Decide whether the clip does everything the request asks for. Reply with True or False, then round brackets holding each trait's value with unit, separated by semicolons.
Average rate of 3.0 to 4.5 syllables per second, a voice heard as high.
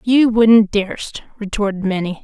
True (4.0 syllables/s; 210 Hz)